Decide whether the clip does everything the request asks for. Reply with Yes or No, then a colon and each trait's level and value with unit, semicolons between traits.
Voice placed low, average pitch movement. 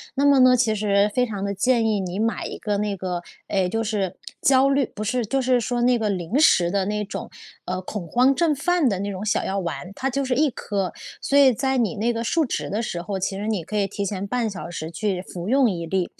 No: high, 210 Hz; average, 4.6 semitones